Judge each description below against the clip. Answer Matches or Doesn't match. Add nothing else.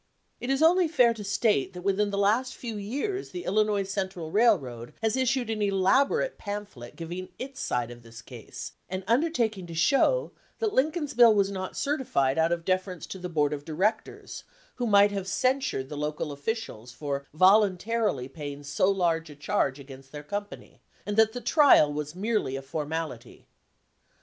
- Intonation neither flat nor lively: Doesn't match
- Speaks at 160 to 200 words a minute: Matches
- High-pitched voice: Matches